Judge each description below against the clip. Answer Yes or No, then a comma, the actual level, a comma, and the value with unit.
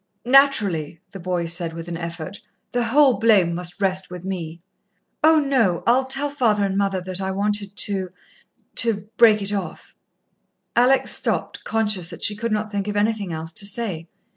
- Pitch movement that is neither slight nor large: Yes, average, 4.2 semitones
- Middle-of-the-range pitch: No, high, 200 Hz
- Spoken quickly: No, average, 175 wpm